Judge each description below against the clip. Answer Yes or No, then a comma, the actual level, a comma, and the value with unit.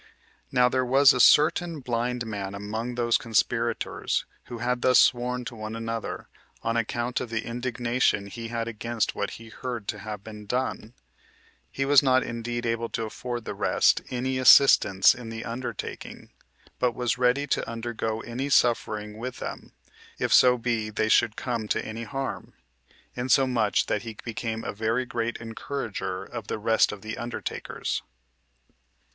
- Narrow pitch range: Yes, narrow, 2.0 semitones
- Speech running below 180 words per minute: Yes, average, 160 wpm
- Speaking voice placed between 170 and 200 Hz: No, low, 115 Hz